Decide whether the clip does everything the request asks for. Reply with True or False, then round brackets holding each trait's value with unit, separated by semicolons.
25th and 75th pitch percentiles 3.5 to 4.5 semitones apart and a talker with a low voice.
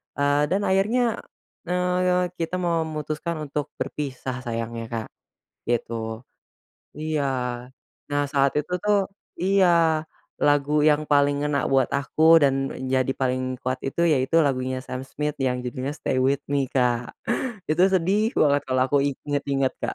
False (3.9 semitones; 145 Hz)